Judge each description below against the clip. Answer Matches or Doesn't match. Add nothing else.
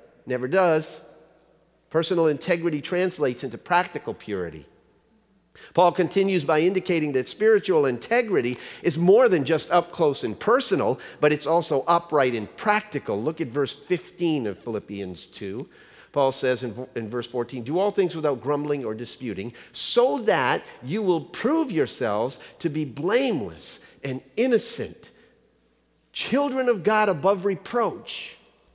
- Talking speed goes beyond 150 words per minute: Doesn't match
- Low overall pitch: Doesn't match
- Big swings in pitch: Matches